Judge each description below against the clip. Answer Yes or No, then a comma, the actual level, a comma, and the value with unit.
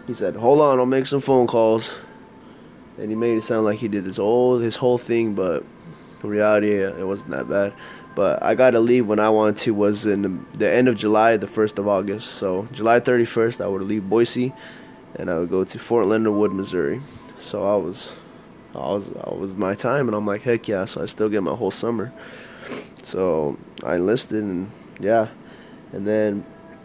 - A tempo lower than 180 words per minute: No, fast, 205 wpm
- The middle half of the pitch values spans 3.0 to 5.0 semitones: No, narrow, 2.6 semitones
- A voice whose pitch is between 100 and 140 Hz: Yes, low, 110 Hz